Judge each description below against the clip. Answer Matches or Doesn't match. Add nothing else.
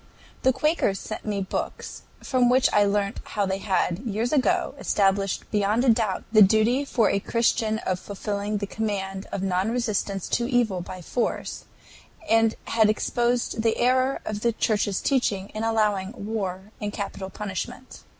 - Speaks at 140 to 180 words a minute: Matches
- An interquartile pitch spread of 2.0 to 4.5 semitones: Matches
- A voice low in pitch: Doesn't match